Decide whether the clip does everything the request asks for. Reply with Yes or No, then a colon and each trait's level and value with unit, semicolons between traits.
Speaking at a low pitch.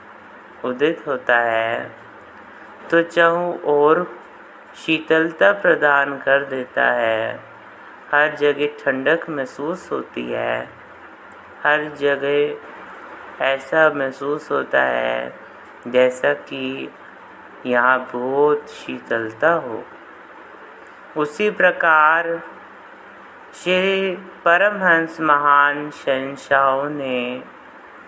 No: medium, 145 Hz